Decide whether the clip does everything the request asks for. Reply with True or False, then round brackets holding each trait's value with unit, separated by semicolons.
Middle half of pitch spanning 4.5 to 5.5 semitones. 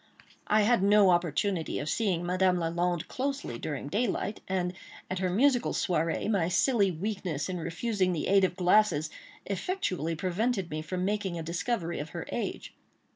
False (3.7 semitones)